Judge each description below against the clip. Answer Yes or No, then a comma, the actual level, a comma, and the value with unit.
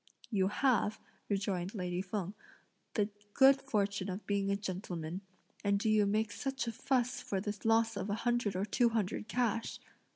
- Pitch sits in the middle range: No, high, 205 Hz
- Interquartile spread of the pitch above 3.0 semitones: No, average, 2.7 semitones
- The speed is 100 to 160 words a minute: No, average, 170 wpm